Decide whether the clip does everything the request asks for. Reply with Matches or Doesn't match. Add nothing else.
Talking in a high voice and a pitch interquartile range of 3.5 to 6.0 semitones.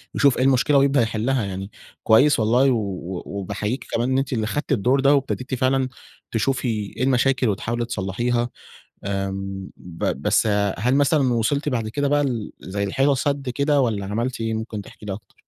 Doesn't match